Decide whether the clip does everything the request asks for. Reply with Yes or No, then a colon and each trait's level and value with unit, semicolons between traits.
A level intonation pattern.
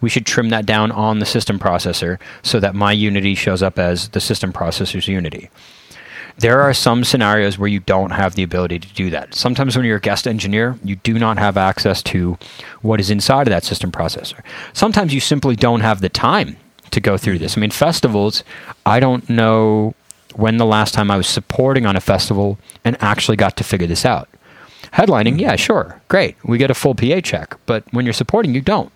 No: average, 3.6 semitones